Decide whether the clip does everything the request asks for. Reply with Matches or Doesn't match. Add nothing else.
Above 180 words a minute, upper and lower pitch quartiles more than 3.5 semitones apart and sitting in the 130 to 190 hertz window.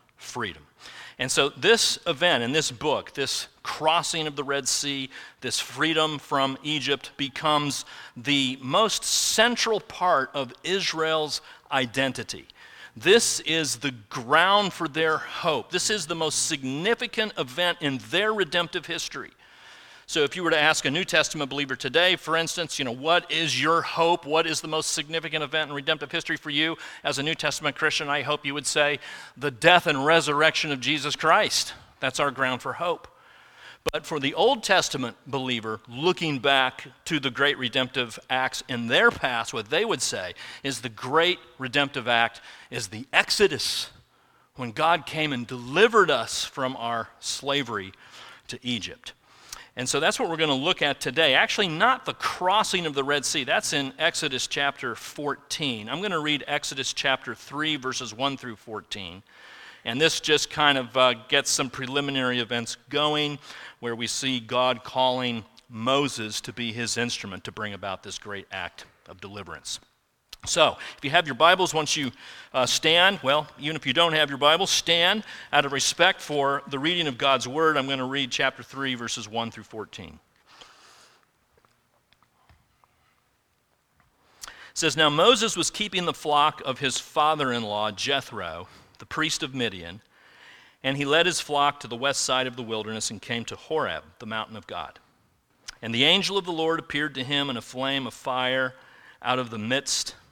Doesn't match